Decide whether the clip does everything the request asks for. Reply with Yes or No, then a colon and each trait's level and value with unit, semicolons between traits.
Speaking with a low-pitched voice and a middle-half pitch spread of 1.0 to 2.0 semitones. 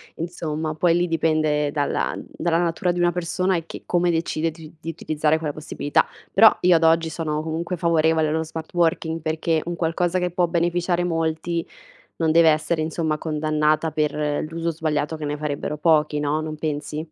No: medium, 160 Hz; narrow, 1.6 semitones